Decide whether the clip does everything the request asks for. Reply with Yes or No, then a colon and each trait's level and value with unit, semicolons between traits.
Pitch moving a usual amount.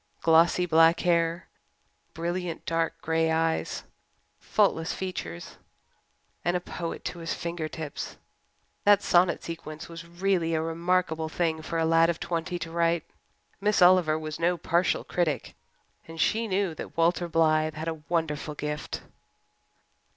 No: narrow, 1.4 semitones